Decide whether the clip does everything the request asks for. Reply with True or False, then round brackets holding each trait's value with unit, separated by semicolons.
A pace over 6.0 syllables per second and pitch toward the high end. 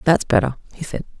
False (6.3 syllables/s; 155 Hz)